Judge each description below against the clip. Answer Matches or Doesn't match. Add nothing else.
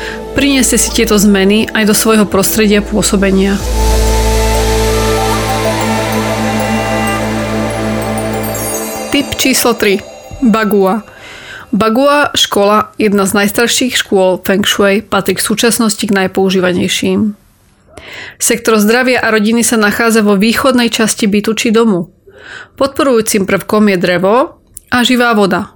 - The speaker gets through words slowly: Matches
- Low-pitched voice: Doesn't match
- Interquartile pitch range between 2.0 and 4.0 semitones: Doesn't match